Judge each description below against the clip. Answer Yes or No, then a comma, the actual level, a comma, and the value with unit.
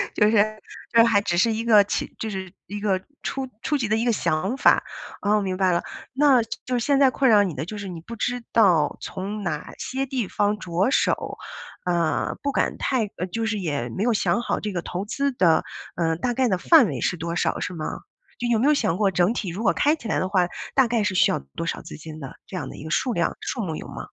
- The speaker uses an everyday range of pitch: Yes, average, 4.9 semitones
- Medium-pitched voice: No, high, 205 Hz